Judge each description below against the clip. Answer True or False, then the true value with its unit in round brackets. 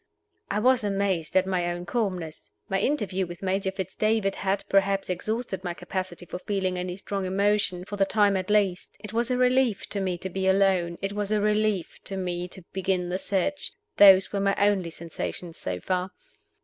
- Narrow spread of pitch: True (2.1 semitones)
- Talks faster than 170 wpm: True (195 wpm)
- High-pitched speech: True (195 Hz)